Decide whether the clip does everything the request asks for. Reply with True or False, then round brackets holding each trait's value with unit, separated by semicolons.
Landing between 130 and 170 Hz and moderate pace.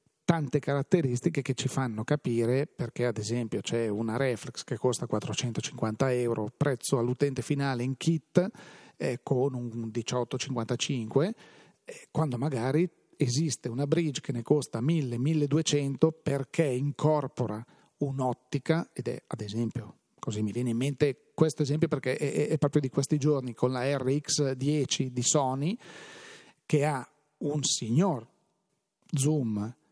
True (140 Hz; 130 wpm)